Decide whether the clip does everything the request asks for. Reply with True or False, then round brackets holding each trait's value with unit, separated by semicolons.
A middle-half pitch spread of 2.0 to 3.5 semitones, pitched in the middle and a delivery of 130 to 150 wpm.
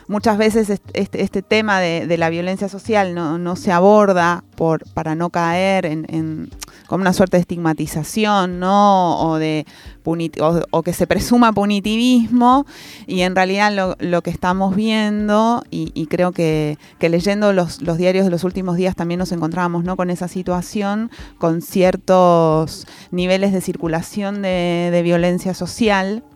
False (2.7 semitones; 180 Hz; 160 wpm)